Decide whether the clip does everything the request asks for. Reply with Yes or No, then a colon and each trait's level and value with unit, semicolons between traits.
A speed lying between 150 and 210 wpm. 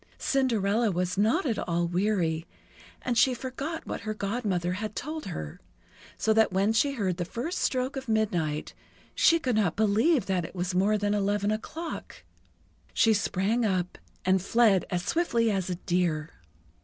Yes: average, 165 wpm